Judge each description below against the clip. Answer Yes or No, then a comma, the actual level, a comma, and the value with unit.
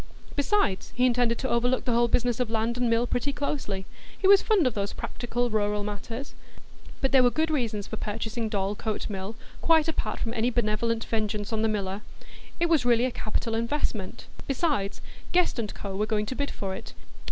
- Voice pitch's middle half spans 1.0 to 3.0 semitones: No, average, 3.4 semitones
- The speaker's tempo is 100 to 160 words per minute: No, average, 190 wpm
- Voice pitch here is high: Yes, high, 230 Hz